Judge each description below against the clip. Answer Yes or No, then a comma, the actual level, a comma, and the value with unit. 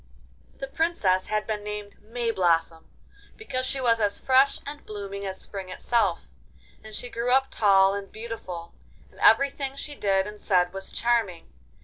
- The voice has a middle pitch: No, high, 210 Hz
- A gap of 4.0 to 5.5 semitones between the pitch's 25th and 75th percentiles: Yes, average, 4.3 semitones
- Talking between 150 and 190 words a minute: Yes, average, 155 wpm